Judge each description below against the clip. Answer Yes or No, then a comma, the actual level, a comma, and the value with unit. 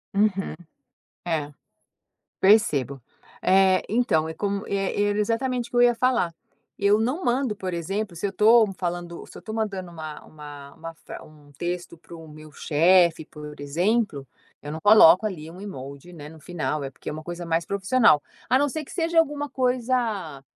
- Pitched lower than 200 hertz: Yes, medium, 185 Hz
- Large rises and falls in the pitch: Yes, wide, 5.8 semitones